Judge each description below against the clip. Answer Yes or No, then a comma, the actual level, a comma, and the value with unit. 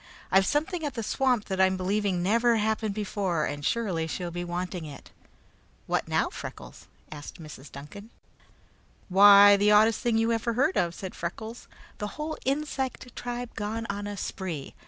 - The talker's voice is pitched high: Yes, high, 205 Hz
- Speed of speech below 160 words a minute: No, average, 165 wpm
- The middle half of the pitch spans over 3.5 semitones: Yes, average, 4.4 semitones